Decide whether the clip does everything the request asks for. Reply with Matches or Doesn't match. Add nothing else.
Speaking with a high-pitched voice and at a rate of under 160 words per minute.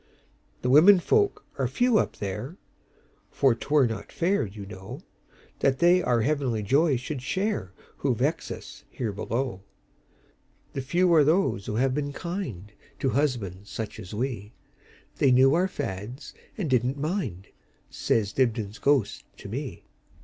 Doesn't match